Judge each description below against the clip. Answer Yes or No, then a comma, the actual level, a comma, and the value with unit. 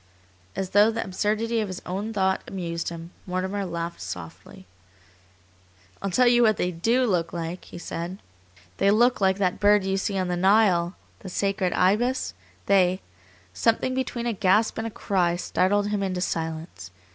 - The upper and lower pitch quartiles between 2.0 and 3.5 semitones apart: Yes, average, 3.1 semitones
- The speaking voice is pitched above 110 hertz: Yes, high, 190 Hz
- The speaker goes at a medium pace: Yes, average, 170 wpm